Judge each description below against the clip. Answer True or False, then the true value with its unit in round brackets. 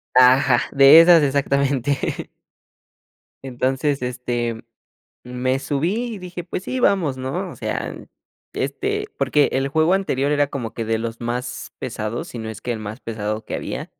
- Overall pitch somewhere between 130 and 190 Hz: True (135 Hz)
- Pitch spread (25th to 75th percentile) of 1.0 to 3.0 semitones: False (4.0 semitones)